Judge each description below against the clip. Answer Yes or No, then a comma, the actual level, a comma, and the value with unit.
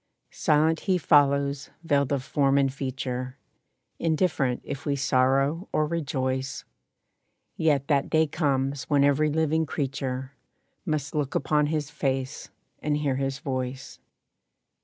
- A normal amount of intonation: No, narrow, 2.1 semitones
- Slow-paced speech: Yes, slow, 125 wpm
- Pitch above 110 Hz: Yes, medium, 140 Hz